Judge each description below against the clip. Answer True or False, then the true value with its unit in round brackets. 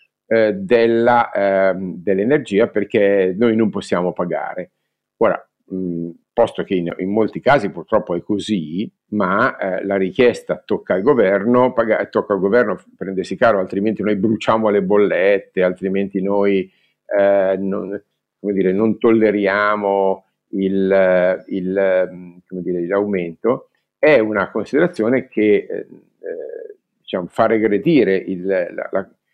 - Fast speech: False (125 wpm)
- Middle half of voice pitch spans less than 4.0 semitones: True (2.6 semitones)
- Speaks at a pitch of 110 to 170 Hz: False (100 Hz)